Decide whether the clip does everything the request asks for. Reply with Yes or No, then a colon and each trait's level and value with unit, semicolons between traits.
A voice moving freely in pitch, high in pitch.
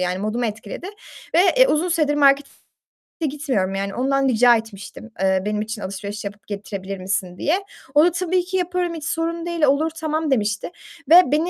Yes: wide, 8.0 semitones; very high, 260 Hz